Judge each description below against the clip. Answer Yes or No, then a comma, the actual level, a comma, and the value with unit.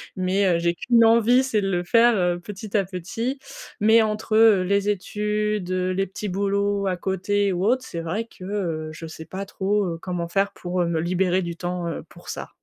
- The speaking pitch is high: Yes, high, 195 Hz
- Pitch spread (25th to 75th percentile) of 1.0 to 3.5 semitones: Yes, average, 2.9 semitones